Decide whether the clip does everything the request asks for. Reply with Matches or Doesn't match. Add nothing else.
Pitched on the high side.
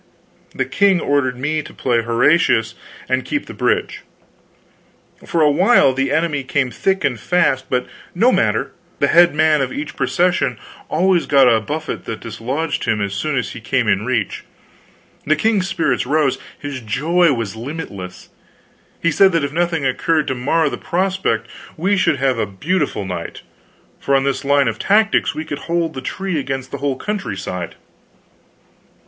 Doesn't match